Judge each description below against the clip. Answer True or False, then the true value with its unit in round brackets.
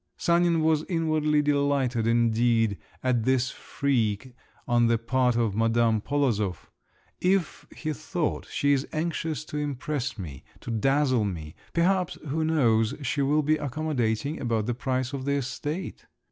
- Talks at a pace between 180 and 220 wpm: False (145 wpm)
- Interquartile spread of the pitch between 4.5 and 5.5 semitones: True (4.8 semitones)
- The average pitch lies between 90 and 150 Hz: True (135 Hz)